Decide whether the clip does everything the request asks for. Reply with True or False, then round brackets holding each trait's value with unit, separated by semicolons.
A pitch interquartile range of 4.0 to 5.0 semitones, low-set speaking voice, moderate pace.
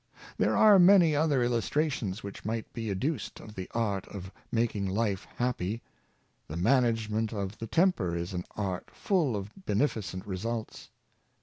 True (4.4 semitones; 110 Hz; 150 wpm)